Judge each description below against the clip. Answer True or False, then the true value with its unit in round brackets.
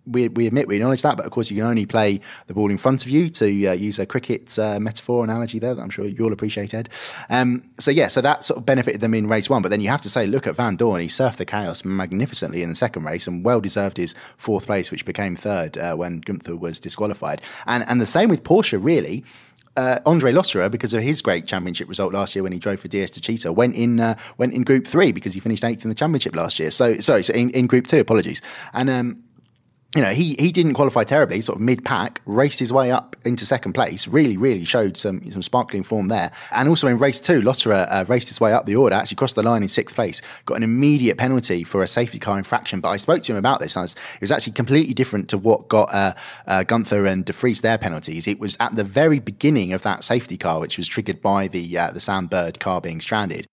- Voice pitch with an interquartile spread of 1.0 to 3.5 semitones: False (4.2 semitones)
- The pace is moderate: False (255 wpm)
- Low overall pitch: True (115 Hz)